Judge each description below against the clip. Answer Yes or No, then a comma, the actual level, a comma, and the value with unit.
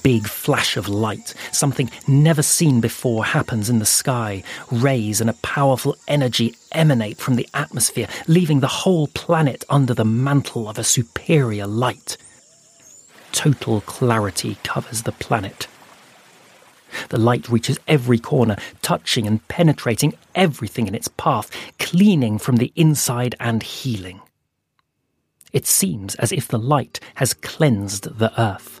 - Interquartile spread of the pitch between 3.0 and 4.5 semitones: Yes, average, 3.9 semitones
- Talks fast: No, slow, 135 wpm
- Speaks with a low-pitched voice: Yes, low, 120 Hz